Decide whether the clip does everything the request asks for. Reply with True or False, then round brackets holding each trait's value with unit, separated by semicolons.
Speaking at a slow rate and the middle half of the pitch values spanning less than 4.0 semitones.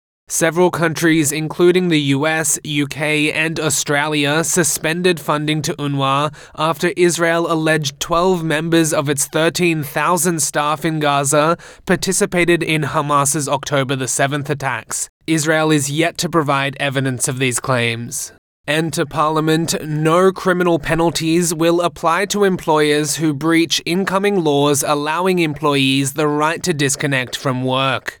True (130 wpm; 2.6 semitones)